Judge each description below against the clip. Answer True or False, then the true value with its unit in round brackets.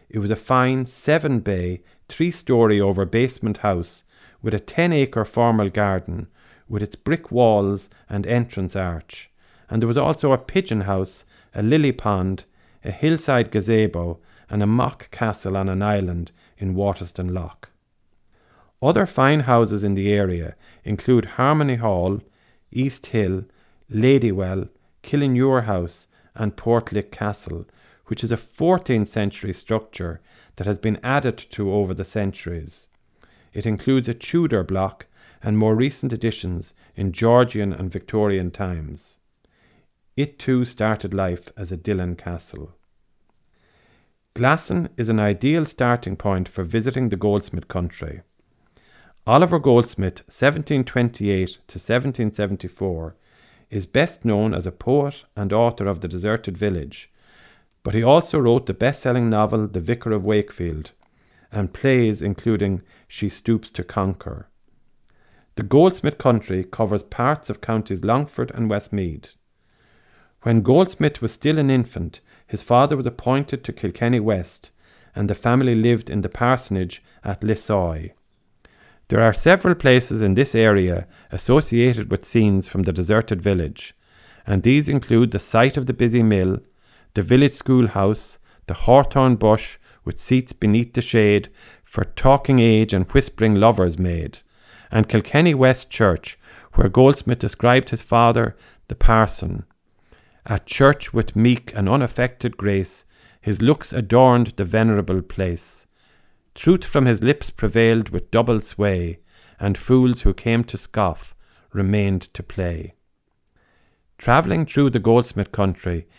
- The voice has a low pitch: True (110 Hz)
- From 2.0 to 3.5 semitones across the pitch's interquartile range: False (4.3 semitones)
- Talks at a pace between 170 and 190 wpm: False (140 wpm)